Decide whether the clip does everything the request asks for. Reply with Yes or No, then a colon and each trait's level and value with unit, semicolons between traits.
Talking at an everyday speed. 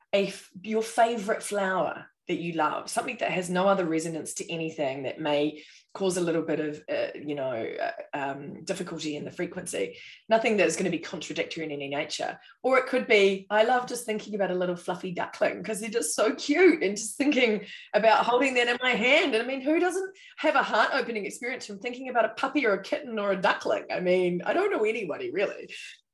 No: fast, 220 wpm